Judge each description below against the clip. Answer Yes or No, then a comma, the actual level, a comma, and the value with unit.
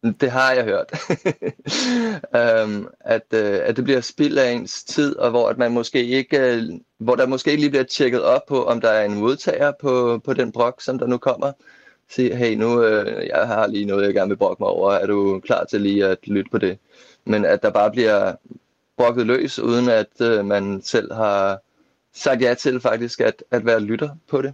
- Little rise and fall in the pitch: No, average, 3.4 semitones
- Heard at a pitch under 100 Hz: No, low, 120 Hz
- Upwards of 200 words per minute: Yes, average, 220 wpm